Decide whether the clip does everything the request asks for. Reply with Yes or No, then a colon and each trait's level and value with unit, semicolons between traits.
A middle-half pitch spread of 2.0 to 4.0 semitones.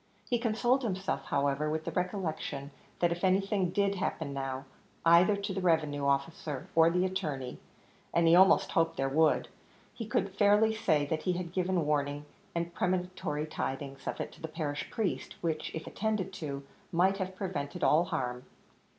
No: average, 4.4 semitones